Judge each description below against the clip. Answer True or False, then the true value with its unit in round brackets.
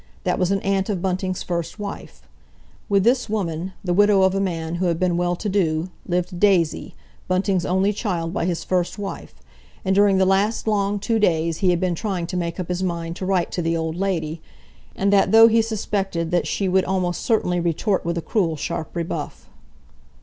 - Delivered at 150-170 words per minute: False (205 wpm)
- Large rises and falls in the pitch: False (2.6 semitones)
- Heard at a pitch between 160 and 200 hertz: True (185 Hz)